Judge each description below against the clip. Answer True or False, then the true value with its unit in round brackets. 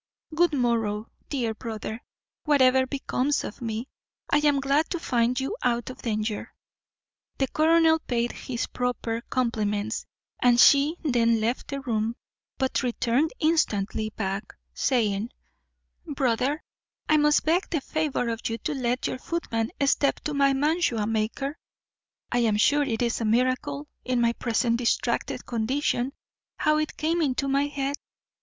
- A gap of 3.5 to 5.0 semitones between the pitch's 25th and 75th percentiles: True (4.0 semitones)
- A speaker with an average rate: True (150 wpm)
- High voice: True (250 Hz)